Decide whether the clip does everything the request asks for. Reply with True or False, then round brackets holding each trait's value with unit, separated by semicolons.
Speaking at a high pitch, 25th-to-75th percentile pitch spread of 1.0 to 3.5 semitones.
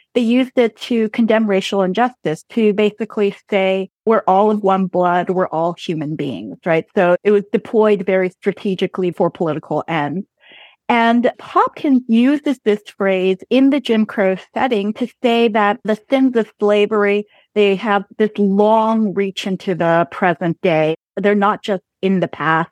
True (205 Hz; 3.1 semitones)